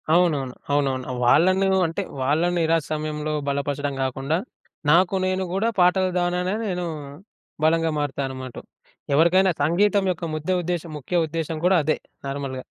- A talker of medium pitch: Yes, medium, 160 Hz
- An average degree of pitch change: Yes, average, 4.0 semitones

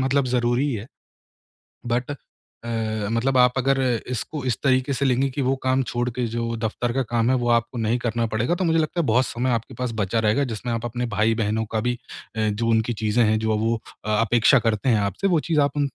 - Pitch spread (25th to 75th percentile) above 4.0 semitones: No, average, 2.7 semitones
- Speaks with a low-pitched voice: Yes, low, 120 Hz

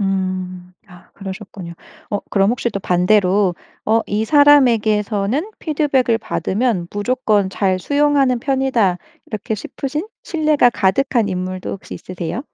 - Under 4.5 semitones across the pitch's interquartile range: No, wide, 5.5 semitones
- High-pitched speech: Yes, high, 210 Hz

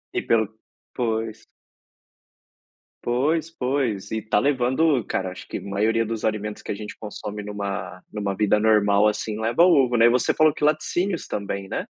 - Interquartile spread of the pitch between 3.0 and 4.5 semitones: Yes, average, 3.7 semitones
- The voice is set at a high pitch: No, low, 110 Hz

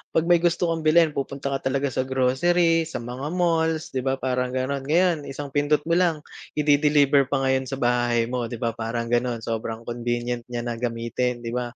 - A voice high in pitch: No, low, 130 Hz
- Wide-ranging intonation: No, average, 4.1 semitones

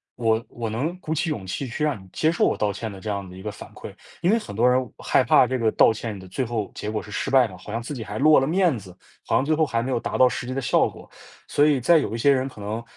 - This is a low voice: Yes, low, 120 Hz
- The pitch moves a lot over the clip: No, average, 4.9 semitones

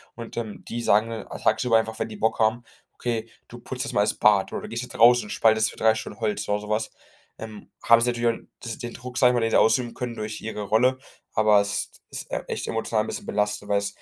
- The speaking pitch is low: Yes, low, 110 Hz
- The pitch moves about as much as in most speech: No, narrow, 1.8 semitones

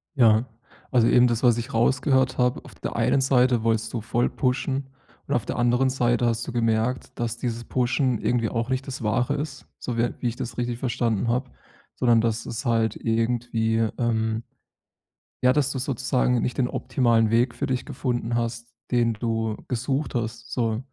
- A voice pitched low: Yes, low, 120 Hz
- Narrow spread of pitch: Yes, narrow, 1.9 semitones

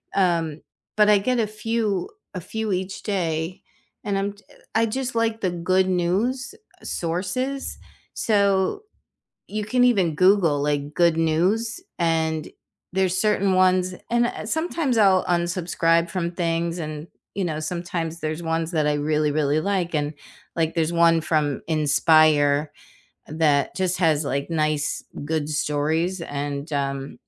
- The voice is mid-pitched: Yes, medium, 170 Hz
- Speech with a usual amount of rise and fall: Yes, average, 4.2 semitones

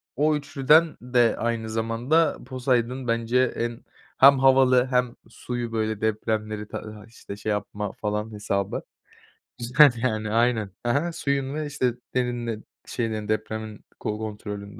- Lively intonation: No, average, 3.1 semitones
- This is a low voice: Yes, low, 115 Hz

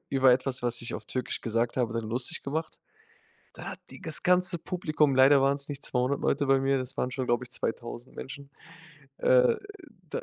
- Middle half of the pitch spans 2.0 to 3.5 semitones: Yes, narrow, 2.4 semitones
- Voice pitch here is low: Yes, low, 130 Hz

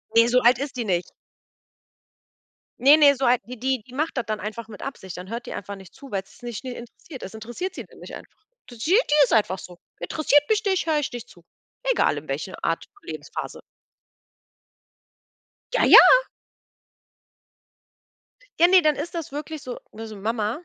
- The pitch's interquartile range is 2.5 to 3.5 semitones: No, average, 5.3 semitones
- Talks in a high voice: Yes, high, 245 Hz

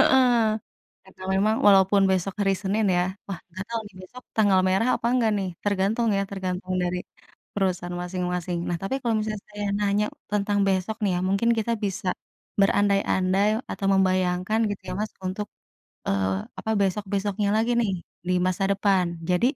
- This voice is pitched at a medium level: No, high, 195 Hz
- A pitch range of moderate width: No, narrow, 2.1 semitones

